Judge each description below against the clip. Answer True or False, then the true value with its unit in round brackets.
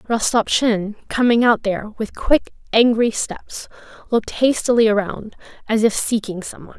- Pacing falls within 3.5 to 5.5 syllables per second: True (4.9 syllables/s)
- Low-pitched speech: False (225 Hz)